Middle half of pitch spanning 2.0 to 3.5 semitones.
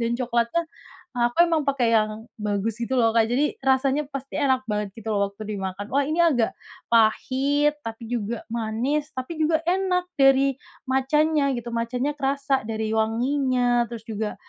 No: average, 3.9 semitones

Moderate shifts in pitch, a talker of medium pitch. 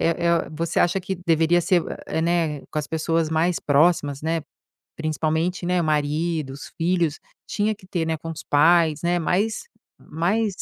No: narrow, 1.9 semitones; medium, 165 Hz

